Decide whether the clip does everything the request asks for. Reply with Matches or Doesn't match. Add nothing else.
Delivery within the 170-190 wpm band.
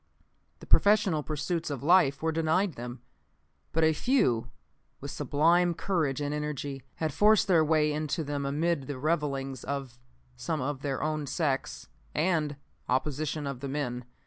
Doesn't match